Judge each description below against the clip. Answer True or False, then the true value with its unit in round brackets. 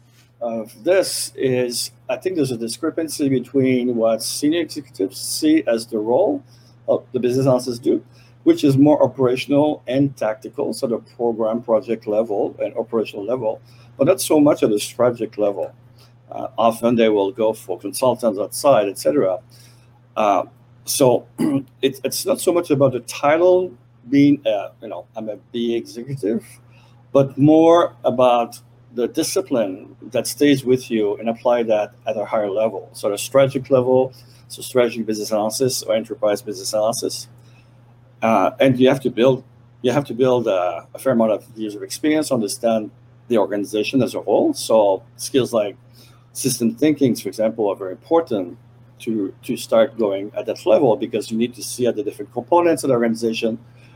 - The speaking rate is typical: True (165 wpm)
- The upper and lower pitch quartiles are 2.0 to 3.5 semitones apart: True (2.5 semitones)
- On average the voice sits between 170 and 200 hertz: False (120 Hz)